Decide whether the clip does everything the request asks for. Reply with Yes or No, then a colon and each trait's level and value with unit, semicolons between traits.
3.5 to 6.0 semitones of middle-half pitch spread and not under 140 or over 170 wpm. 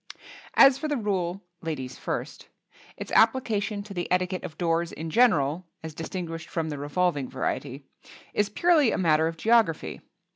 Yes: average, 4.7 semitones; average, 155 wpm